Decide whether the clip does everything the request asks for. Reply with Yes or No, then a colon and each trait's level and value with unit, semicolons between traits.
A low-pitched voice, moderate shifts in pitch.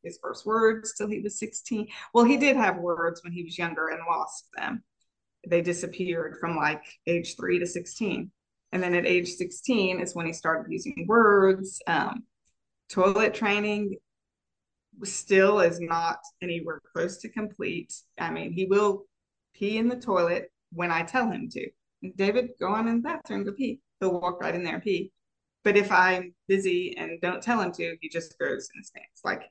No: high, 190 Hz; average, 3.7 semitones